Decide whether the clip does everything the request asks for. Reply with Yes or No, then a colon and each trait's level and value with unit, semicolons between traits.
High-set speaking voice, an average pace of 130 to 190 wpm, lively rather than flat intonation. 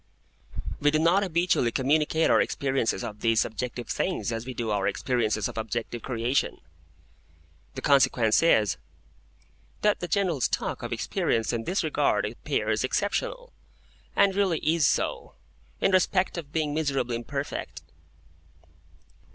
No: medium, 140 Hz; slow, 135 wpm; wide, 6.4 semitones